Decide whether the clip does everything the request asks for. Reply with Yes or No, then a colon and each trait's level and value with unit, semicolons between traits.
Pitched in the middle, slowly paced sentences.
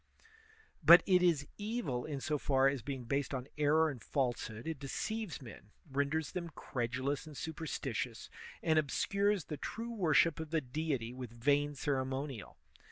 No: medium, 145 Hz; average, 155 wpm